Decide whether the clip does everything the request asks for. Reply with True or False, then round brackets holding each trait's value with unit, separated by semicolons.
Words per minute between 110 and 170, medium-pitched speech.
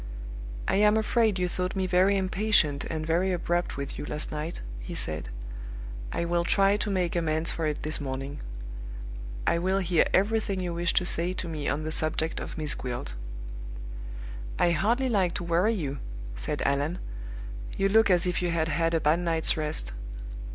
False (180 wpm; 170 Hz)